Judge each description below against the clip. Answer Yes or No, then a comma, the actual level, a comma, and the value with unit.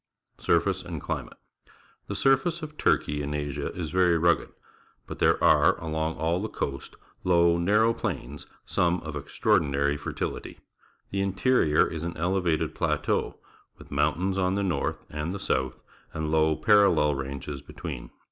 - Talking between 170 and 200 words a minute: No, average, 150 wpm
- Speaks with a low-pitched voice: Yes, very low, 80 Hz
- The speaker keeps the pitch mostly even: No, average, 4.4 semitones